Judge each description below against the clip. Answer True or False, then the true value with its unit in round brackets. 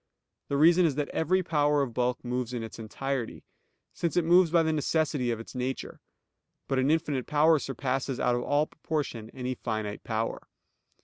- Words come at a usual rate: True (180 wpm)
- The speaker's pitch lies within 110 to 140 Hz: True (135 Hz)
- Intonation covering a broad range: False (4.2 semitones)